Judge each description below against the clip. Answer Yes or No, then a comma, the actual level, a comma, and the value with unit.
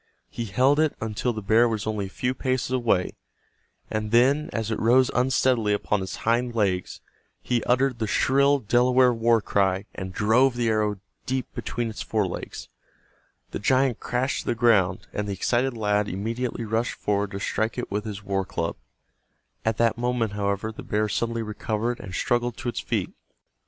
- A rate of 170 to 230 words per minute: Yes, average, 180 wpm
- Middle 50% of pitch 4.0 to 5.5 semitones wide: No, average, 3.0 semitones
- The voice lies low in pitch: Yes, low, 115 Hz